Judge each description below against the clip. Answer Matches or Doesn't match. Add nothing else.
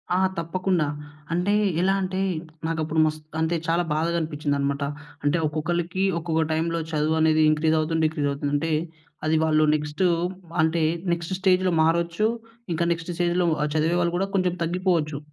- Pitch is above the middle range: Doesn't match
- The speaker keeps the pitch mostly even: Matches